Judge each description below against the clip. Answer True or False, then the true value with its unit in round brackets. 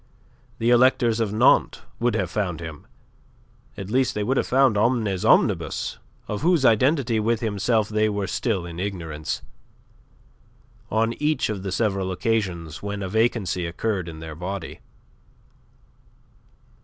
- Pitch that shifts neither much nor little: True (4.1 semitones)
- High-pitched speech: False (105 Hz)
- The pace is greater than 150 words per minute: False (140 wpm)